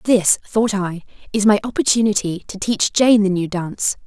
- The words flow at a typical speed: Yes, average, 175 wpm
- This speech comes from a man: No, female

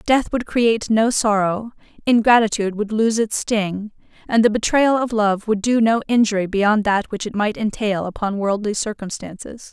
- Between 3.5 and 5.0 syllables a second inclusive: Yes, 4.9 syllables/s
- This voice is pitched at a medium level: No, high, 215 Hz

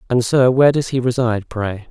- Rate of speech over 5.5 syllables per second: Yes, 6.0 syllables/s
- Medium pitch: No, low, 120 Hz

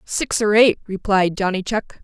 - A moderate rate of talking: Yes, average, 175 wpm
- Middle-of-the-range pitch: No, high, 200 Hz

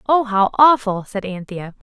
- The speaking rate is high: No, average, 155 wpm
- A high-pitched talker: Yes, high, 220 Hz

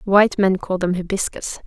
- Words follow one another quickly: No, average, 180 wpm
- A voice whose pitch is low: No, high, 190 Hz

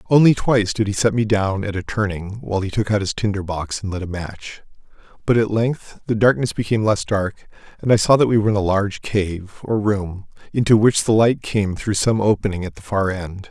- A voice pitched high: No, low, 105 Hz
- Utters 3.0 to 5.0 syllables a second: No, 5.5 syllables/s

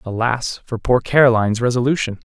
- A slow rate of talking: Yes, slow, 130 wpm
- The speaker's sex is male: Yes, male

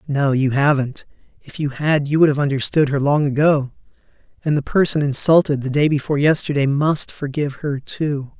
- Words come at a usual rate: Yes, average, 170 wpm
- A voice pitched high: No, medium, 145 Hz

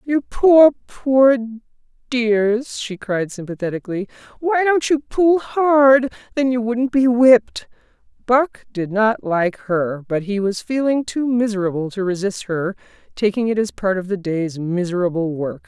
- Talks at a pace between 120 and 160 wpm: Yes, average, 150 wpm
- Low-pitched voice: No, high, 220 Hz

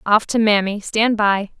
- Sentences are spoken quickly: No, average, 190 wpm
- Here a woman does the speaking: Yes, female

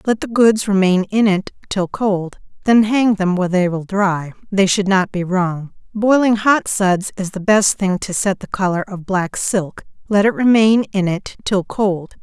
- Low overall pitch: No, high, 195 Hz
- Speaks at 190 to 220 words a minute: Yes, average, 195 wpm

